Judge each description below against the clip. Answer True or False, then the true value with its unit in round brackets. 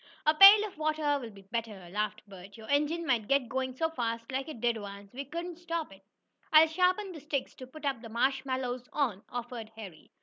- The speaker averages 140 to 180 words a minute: False (205 wpm)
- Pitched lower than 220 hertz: False (260 Hz)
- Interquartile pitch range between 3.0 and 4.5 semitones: False (5.6 semitones)